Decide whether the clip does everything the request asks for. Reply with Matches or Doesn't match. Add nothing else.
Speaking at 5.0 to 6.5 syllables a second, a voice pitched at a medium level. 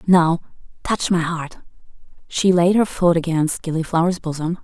Doesn't match